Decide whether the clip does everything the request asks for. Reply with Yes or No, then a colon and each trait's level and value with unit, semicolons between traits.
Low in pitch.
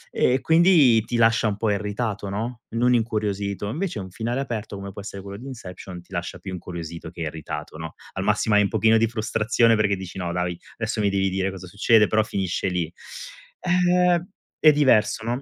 Yes: low, 105 Hz